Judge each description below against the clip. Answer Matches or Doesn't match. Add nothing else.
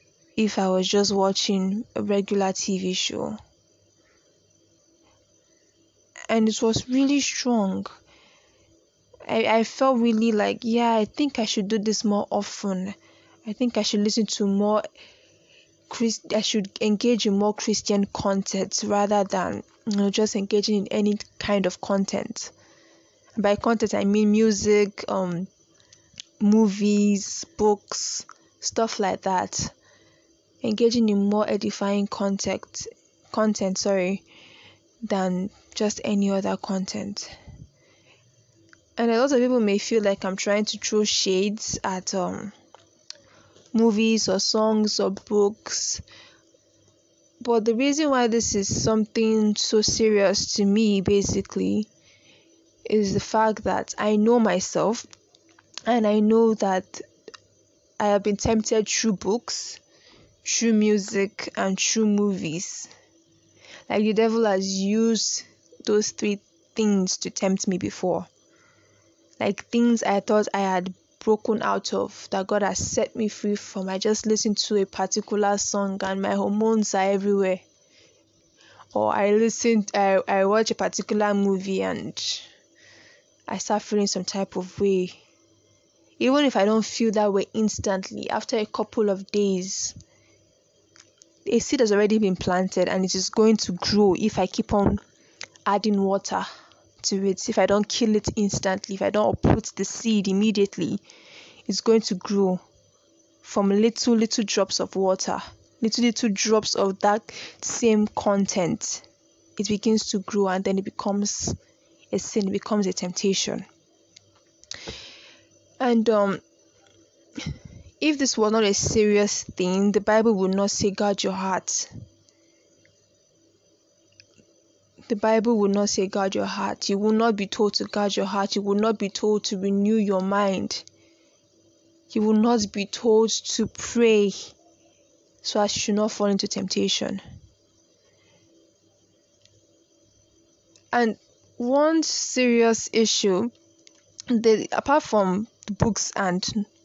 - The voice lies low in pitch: Doesn't match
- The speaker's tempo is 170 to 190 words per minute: Doesn't match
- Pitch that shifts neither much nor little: Doesn't match